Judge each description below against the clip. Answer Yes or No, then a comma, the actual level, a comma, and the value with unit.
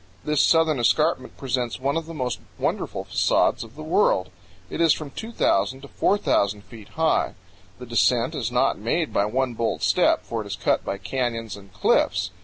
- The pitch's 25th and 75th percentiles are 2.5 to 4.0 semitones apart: No, average, 5.2 semitones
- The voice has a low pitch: Yes, low, 125 Hz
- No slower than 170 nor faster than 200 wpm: Yes, average, 185 wpm